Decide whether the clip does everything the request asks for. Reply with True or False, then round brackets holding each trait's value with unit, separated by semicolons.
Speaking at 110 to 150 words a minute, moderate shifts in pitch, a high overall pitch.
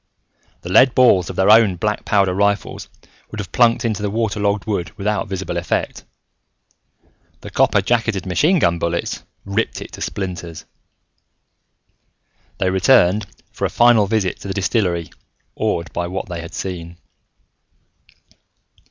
False (145 wpm; 3.4 semitones; 100 Hz)